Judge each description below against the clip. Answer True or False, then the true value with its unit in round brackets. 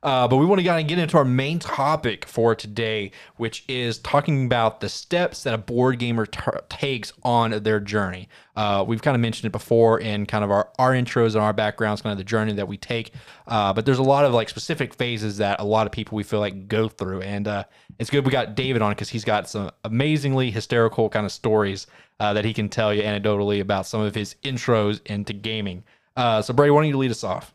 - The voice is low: True (110 Hz)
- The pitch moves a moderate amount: True (3.3 semitones)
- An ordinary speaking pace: False (240 wpm)